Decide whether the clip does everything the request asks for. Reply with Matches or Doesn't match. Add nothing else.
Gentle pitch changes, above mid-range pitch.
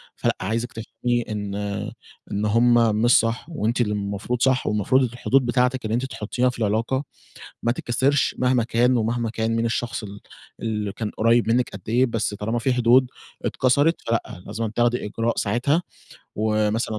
Doesn't match